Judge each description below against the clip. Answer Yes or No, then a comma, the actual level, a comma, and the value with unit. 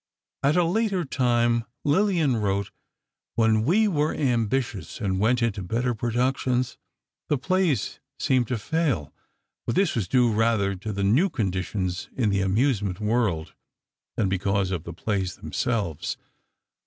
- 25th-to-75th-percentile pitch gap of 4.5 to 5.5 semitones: Yes, average, 5.2 semitones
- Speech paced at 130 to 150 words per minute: Yes, average, 140 wpm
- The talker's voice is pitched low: Yes, low, 115 Hz